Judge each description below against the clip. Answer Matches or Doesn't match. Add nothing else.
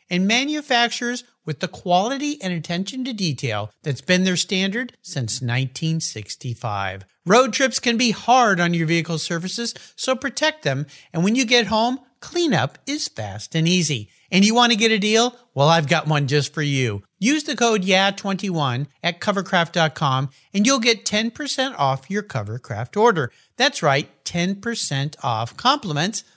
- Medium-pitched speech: Matches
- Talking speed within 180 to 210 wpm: Doesn't match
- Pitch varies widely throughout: Matches